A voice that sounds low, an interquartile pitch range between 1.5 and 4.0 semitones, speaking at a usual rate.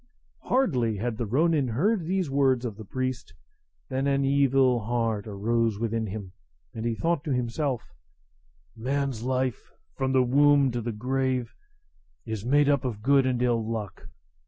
Yes: low, 125 Hz; average, 3.3 semitones; average, 160 wpm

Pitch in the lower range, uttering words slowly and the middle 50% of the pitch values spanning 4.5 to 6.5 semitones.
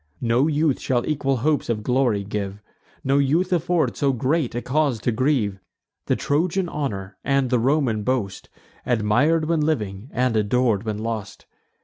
No: low, 130 Hz; average, 155 wpm; wide, 5.4 semitones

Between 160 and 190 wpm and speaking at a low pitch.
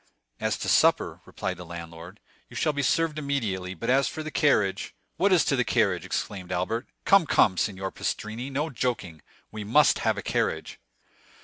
Yes: average, 180 wpm; low, 115 Hz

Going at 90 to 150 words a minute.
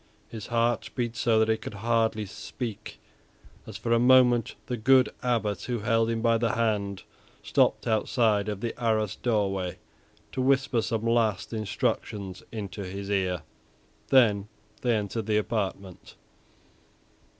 Yes: average, 140 wpm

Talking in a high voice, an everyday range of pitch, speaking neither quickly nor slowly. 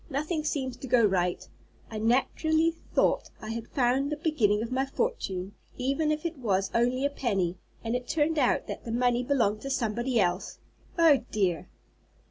Yes: very high, 250 Hz; average, 4.9 semitones; average, 175 wpm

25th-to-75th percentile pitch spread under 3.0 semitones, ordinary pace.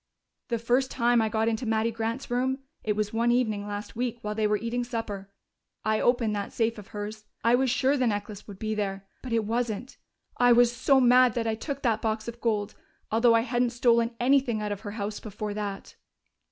No: narrow, 2.4 semitones; fast, 215 wpm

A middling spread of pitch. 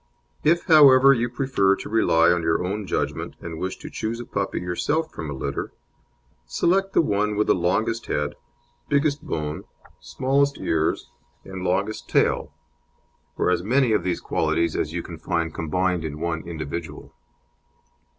No: wide, 6.8 semitones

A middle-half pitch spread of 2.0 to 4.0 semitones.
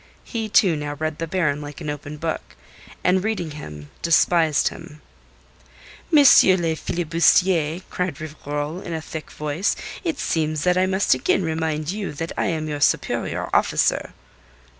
Yes: average, 3.3 semitones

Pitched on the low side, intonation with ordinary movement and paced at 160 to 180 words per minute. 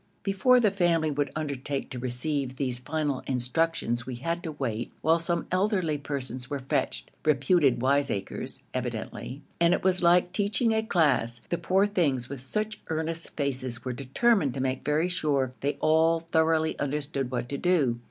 No: medium, 150 Hz; average, 4.7 semitones; average, 165 wpm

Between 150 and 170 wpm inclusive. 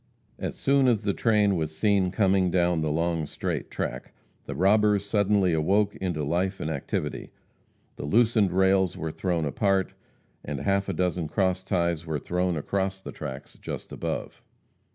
Yes: average, 160 wpm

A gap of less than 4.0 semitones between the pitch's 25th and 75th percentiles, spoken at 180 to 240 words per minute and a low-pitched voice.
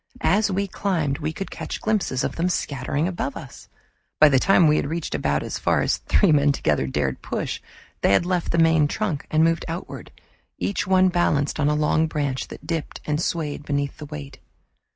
No: average, 3.4 semitones; average, 200 wpm; medium, 155 Hz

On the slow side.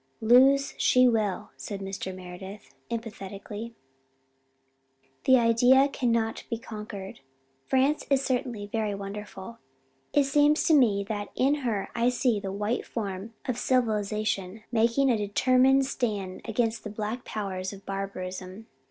Yes: slow, 130 wpm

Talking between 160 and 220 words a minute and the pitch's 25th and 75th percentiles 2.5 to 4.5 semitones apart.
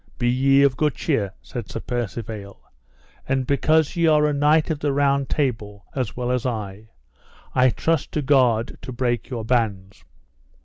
Yes: average, 170 wpm; average, 4.0 semitones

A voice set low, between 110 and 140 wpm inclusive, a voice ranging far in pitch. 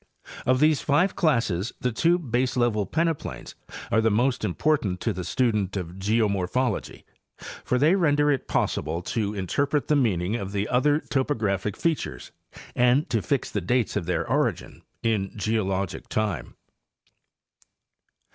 Yes: low, 115 Hz; slow, 135 wpm; wide, 6.0 semitones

